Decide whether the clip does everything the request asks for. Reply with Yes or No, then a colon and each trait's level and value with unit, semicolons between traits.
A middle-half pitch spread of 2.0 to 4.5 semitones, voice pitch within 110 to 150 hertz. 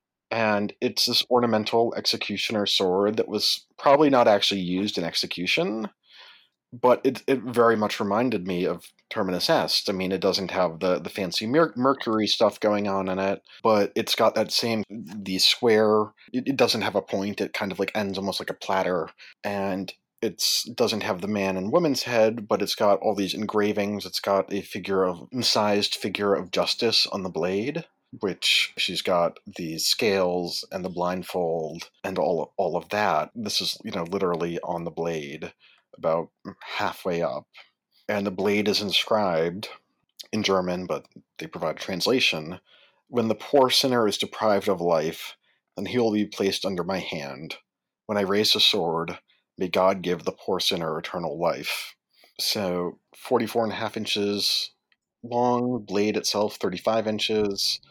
No: average, 2.7 semitones; low, 100 Hz